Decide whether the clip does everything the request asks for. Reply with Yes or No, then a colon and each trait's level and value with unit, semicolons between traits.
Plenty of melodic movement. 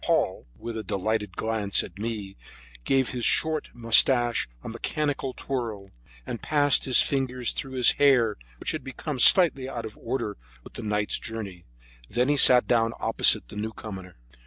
No: average, 3.7 semitones